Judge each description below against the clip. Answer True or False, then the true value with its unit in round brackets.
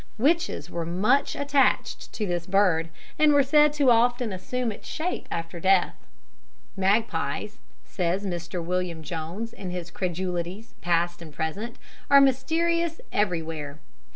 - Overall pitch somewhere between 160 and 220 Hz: True (190 Hz)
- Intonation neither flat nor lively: False (6.7 semitones)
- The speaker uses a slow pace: True (130 wpm)